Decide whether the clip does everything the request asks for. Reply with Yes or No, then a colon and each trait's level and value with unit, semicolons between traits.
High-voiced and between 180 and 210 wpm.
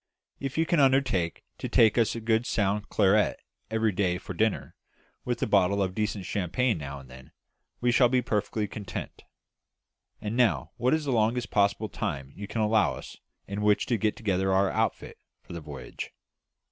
No: low, 105 Hz; average, 185 wpm